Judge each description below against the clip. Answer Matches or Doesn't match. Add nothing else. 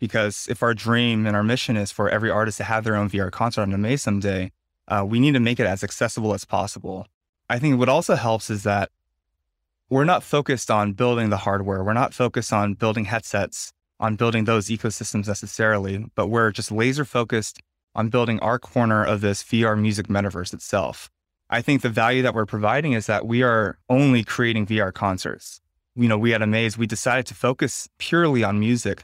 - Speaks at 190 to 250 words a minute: Matches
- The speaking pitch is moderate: Doesn't match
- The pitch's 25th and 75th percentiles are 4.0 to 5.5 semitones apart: Doesn't match